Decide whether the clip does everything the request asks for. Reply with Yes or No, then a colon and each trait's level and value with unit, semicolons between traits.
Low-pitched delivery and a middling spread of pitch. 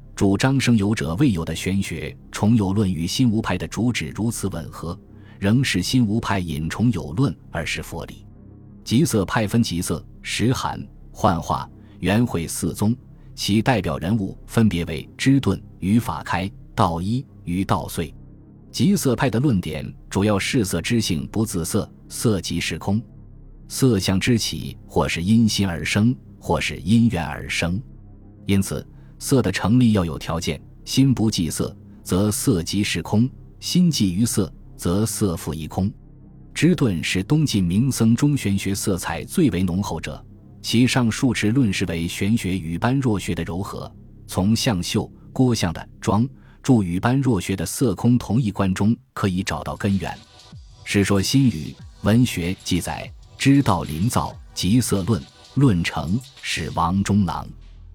Yes: low, 105 Hz; average, 4.9 semitones